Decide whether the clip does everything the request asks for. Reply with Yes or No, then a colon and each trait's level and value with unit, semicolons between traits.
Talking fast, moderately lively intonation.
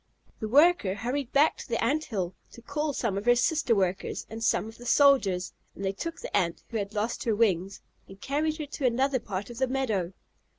No: fast, 220 wpm; wide, 5.8 semitones